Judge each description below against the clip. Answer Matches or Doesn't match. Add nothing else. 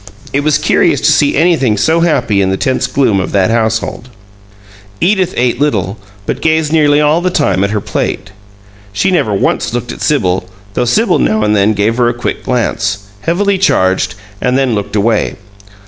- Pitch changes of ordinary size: Doesn't match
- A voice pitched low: Matches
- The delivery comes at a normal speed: Matches